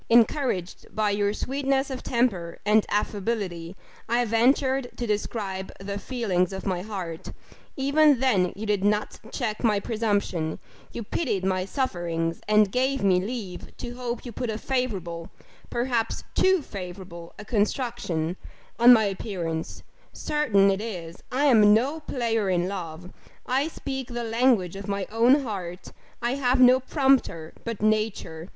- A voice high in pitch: Yes, high, 215 Hz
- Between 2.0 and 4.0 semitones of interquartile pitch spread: No, average, 4.8 semitones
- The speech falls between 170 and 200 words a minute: No, average, 145 wpm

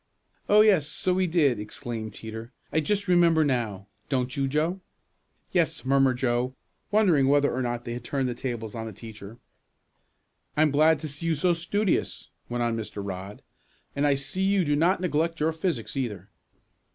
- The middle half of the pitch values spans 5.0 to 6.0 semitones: Yes, wide, 5.6 semitones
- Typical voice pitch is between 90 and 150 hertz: Yes, medium, 140 Hz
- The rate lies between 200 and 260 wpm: No, average, 180 wpm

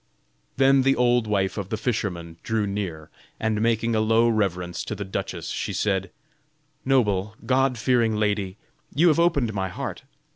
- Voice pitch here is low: Yes, low, 110 Hz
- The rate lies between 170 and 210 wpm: No, average, 160 wpm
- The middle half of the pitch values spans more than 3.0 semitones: Yes, average, 3.8 semitones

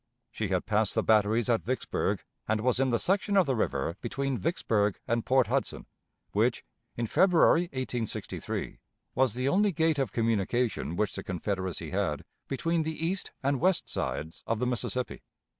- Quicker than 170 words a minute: No, average, 165 wpm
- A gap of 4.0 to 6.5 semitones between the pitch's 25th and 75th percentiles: Yes, average, 5.1 semitones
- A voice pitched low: Yes, low, 120 Hz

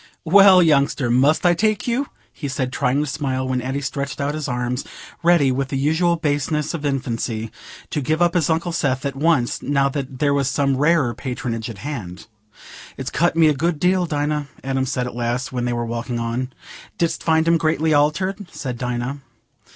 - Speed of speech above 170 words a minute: Yes, average, 190 wpm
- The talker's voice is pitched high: No, medium, 140 Hz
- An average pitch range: Yes, average, 4.0 semitones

